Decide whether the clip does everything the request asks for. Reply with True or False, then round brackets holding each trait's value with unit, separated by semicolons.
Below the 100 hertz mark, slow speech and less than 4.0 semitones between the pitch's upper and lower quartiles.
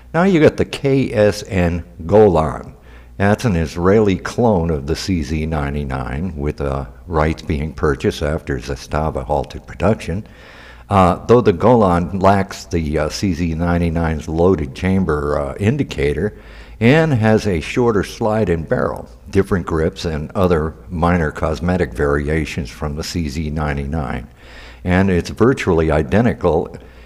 False (85 Hz; 120 wpm; 4.4 semitones)